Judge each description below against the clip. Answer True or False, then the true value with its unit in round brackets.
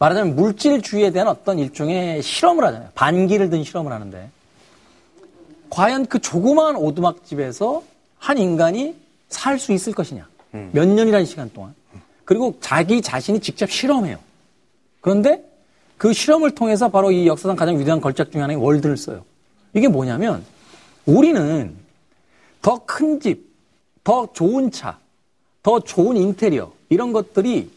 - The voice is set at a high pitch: True (195 Hz)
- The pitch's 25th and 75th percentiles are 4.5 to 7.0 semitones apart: False (8.3 semitones)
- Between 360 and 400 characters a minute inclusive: False (300 characters per minute)